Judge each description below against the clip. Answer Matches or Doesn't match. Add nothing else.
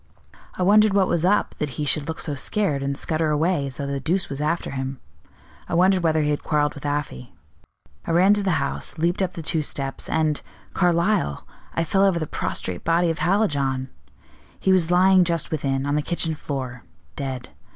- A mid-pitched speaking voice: Matches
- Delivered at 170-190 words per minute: Doesn't match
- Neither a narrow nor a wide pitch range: Matches